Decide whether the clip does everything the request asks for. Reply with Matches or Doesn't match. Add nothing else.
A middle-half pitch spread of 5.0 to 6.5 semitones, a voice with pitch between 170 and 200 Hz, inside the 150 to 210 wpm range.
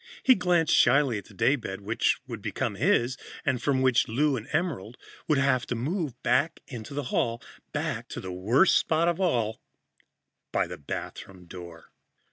Doesn't match